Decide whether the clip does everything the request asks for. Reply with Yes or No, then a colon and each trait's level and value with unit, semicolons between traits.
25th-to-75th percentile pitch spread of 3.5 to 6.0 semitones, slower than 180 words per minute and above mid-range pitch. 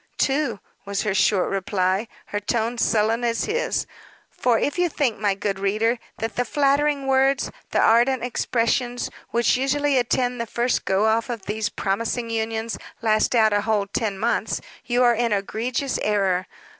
No: average, 3.1 semitones; average, 165 wpm; high, 230 Hz